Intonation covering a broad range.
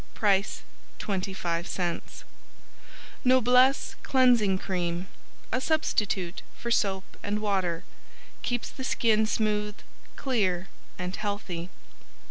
No: average, 4.2 semitones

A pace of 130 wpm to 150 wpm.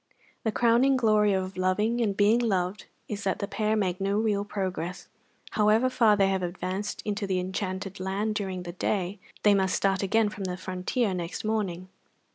No: average, 180 wpm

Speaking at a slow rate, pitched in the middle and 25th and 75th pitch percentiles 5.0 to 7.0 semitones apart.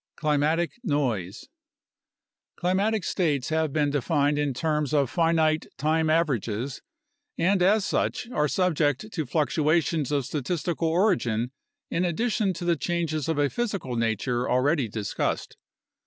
No: slow, 125 wpm; medium, 155 Hz; average, 3.6 semitones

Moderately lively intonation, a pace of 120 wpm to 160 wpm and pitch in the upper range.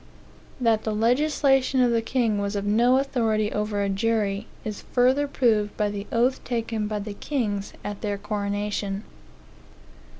Yes: average, 3.1 semitones; average, 155 wpm; high, 215 Hz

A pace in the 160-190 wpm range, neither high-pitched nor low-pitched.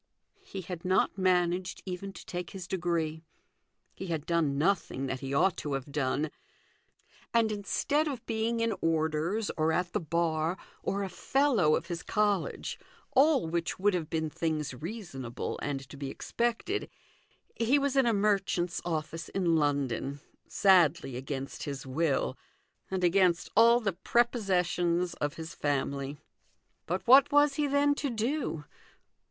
No: average, 150 wpm; medium, 175 Hz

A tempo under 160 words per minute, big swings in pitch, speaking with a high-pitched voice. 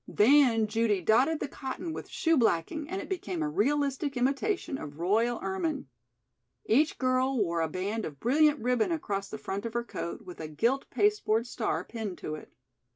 No: average, 180 wpm; wide, 6.4 semitones; high, 235 Hz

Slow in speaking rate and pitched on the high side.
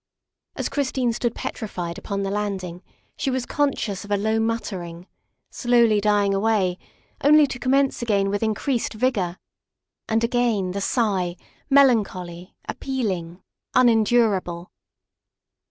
Yes: slow, 120 wpm; high, 215 Hz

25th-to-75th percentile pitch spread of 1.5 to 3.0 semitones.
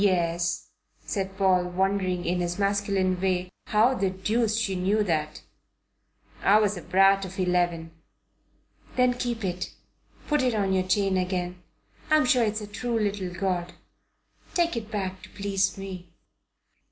Yes: narrow, 2.6 semitones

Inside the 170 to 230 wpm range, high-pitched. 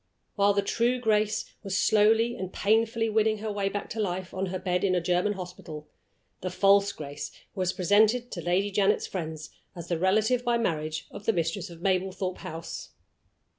Yes: average, 180 wpm; high, 195 Hz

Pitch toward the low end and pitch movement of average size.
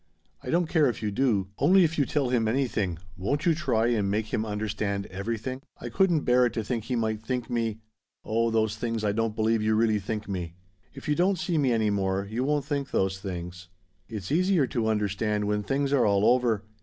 Yes: low, 115 Hz; average, 4.3 semitones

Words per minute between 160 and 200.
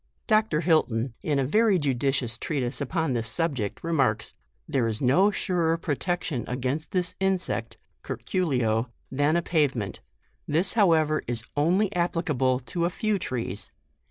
No: average, 150 wpm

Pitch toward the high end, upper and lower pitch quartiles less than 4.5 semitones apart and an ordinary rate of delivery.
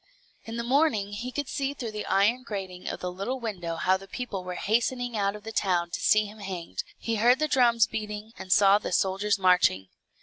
No: high, 210 Hz; average, 3.8 semitones; fast, 215 wpm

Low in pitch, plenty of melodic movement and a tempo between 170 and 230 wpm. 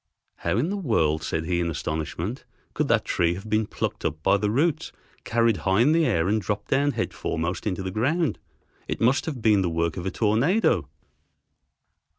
Yes: low, 105 Hz; wide, 6.4 semitones; average, 195 wpm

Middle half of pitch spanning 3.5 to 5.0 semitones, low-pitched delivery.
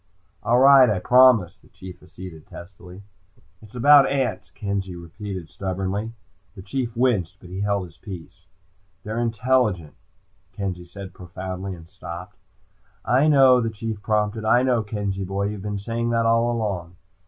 Yes: average, 4.0 semitones; low, 100 Hz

